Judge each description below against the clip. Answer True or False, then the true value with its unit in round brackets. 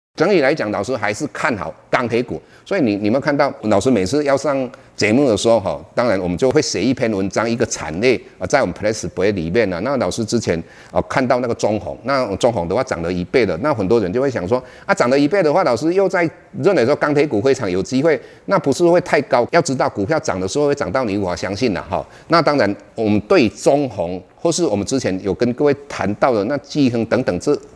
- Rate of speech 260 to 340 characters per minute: False (360 characters per minute)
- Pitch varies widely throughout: True (6.2 semitones)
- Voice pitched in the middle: False (125 Hz)